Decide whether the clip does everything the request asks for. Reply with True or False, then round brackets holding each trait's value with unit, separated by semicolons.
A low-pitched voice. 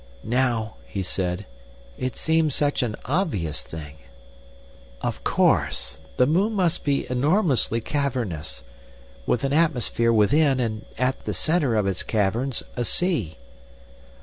True (125 Hz)